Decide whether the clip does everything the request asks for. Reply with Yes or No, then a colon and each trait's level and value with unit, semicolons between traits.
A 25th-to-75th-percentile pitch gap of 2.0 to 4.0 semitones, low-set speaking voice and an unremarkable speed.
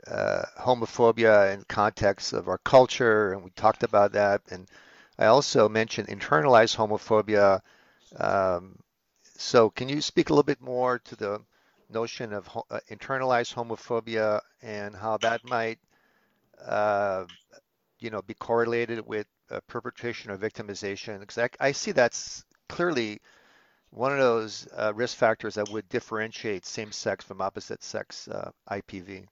Yes: narrow, 2.6 semitones; low, 110 Hz; average, 145 wpm